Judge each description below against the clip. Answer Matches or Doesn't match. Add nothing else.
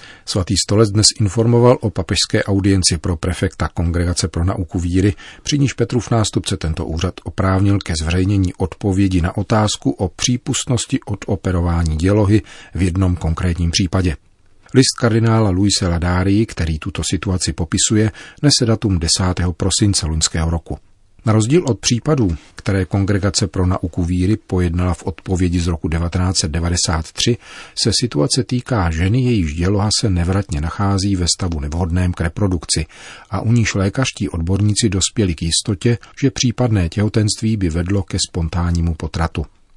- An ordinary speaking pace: Matches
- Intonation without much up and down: Doesn't match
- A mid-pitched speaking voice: Doesn't match